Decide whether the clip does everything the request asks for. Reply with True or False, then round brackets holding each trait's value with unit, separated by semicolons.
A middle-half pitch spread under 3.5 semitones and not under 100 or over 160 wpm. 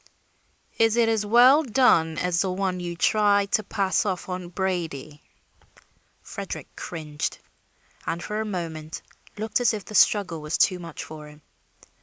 False (4.3 semitones; 155 wpm)